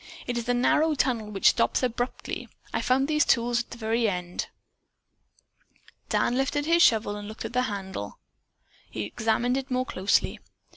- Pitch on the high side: Yes, high, 240 Hz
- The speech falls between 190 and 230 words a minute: No, average, 175 wpm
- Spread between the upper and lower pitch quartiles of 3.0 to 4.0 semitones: Yes, average, 3.4 semitones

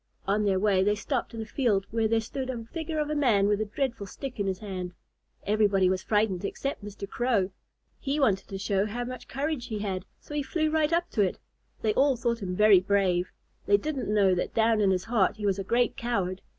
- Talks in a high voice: Yes, high, 215 Hz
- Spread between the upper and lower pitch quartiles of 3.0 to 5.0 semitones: Yes, average, 4.4 semitones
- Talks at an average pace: No, fast, 230 wpm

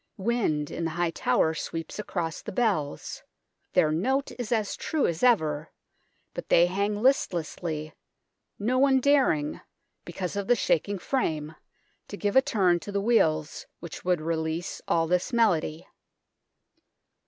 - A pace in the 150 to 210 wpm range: No, average, 140 wpm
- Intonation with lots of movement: Yes, wide, 5.8 semitones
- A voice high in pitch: No, medium, 180 Hz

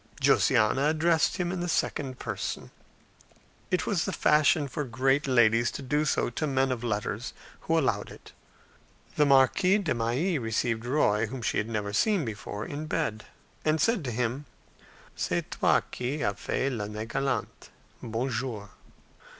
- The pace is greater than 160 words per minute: No, average, 155 wpm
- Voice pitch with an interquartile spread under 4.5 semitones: No, average, 5.2 semitones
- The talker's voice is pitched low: Yes, low, 130 Hz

